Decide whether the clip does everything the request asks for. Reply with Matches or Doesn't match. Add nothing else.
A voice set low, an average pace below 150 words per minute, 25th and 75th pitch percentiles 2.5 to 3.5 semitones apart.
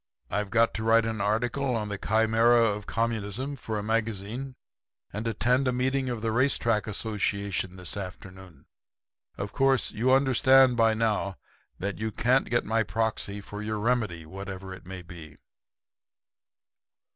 Doesn't match